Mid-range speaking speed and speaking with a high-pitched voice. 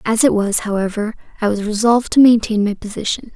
Yes: average, 195 wpm; high, 215 Hz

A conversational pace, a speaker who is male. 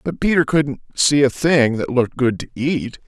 No: fast, 215 wpm; male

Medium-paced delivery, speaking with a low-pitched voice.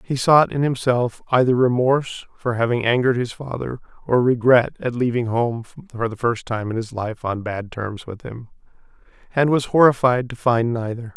Yes: average, 185 wpm; low, 120 Hz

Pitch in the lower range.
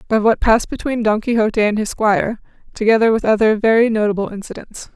No: high, 220 Hz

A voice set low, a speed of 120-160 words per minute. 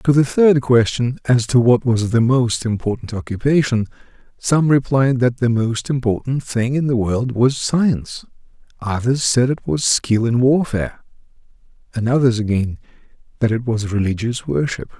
Yes: low, 120 Hz; average, 155 wpm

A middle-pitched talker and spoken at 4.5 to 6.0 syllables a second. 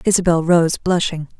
Yes: medium, 170 Hz; 4.9 syllables/s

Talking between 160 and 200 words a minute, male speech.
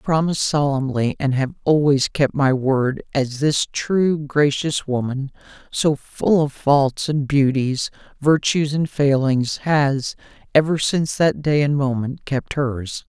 No: average, 145 wpm; male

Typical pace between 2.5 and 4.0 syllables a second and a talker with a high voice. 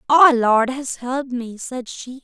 Yes: 3.9 syllables/s; very high, 255 Hz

